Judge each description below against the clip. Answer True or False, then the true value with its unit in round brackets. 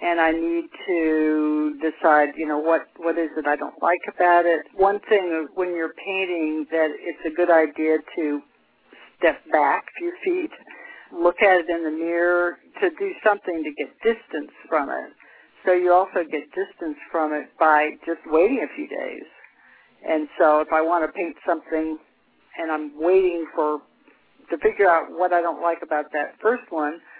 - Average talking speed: True (180 wpm)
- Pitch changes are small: False (3.4 semitones)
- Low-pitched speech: False (170 Hz)